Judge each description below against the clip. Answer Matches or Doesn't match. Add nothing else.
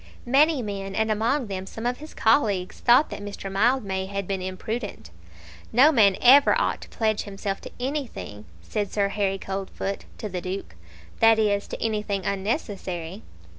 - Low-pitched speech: Doesn't match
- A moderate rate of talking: Matches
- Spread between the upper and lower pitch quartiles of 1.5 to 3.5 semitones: Matches